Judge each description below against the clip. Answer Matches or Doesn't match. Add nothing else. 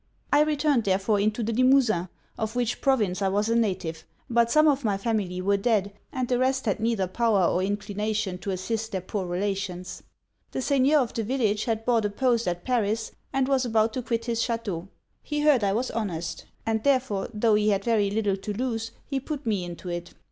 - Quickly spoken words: Matches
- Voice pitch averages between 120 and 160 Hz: Doesn't match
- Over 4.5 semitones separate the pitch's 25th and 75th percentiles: Doesn't match